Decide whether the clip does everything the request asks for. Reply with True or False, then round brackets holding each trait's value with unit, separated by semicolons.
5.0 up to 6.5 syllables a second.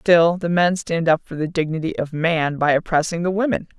True (5.3 syllables/s)